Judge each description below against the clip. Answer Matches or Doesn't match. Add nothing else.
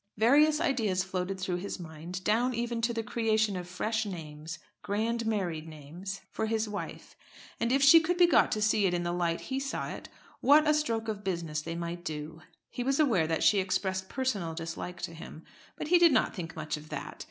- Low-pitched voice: Doesn't match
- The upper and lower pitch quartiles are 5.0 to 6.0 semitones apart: Matches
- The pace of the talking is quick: Matches